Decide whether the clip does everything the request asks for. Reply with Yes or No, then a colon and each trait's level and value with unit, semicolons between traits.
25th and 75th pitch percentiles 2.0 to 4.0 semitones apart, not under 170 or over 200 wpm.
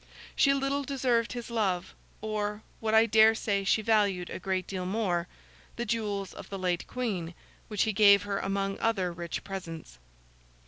No: average, 3.0 semitones; average, 155 wpm